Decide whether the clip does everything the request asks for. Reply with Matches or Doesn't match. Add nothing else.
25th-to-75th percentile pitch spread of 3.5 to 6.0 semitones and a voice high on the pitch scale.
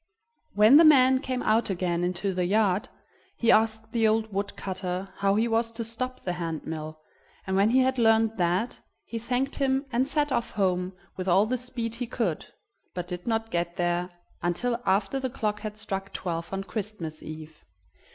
Matches